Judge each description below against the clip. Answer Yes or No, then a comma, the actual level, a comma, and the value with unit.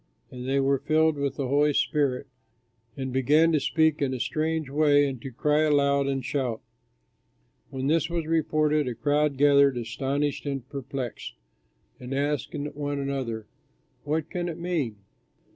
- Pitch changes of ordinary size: No, narrow, 2.3 semitones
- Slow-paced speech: No, average, 155 wpm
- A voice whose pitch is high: No, medium, 140 Hz